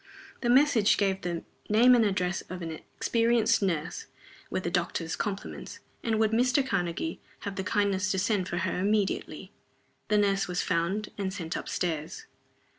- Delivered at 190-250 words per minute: No, average, 165 wpm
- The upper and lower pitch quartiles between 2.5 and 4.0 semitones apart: Yes, average, 3.5 semitones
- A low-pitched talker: No, high, 195 Hz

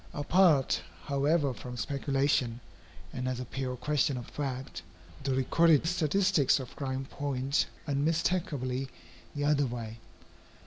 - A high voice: No, medium, 140 Hz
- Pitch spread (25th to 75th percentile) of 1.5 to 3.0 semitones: Yes, narrow, 2.6 semitones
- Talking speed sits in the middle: No, slow, 120 wpm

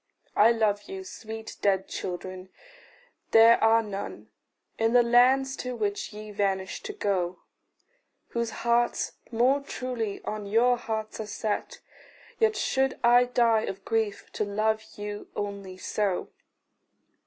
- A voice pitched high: Yes, high, 220 Hz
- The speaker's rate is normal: No, slow, 130 wpm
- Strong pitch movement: No, average, 2.9 semitones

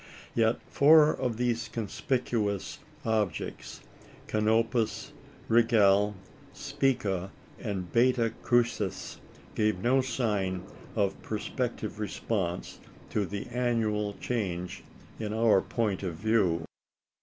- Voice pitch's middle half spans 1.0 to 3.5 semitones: Yes, average, 3.0 semitones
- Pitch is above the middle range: No, low, 110 Hz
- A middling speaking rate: No, slow, 95 wpm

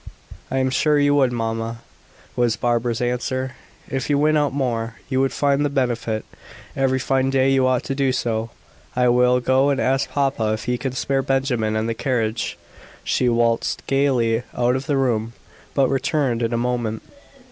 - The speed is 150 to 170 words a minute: No, average, 180 wpm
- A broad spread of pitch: No, narrow, 2.5 semitones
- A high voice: No, low, 125 Hz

